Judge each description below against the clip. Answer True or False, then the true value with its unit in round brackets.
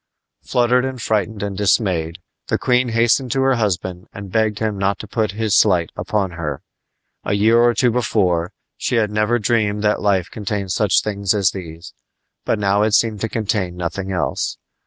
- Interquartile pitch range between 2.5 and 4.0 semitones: True (2.9 semitones)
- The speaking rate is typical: True (180 wpm)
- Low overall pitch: True (105 Hz)